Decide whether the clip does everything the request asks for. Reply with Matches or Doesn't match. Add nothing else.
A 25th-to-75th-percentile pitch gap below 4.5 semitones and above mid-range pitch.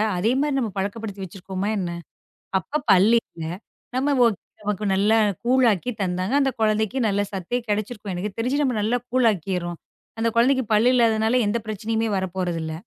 Matches